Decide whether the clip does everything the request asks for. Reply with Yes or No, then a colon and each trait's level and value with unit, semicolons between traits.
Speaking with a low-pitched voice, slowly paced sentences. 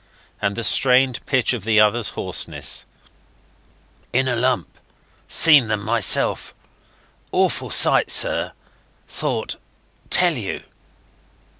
Yes: low, 120 Hz; slow, 105 wpm